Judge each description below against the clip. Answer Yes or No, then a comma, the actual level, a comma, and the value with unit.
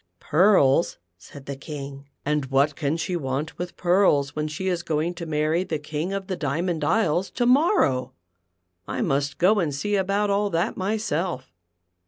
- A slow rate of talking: No, average, 175 wpm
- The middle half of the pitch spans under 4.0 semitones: No, average, 4.7 semitones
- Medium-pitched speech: Yes, medium, 165 Hz